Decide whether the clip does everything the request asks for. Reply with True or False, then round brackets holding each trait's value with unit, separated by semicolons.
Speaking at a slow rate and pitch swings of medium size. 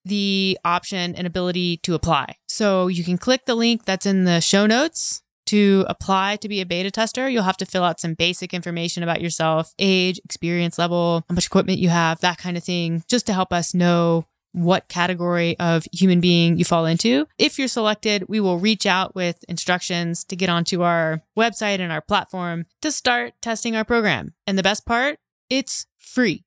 False (195 wpm; 3.2 semitones)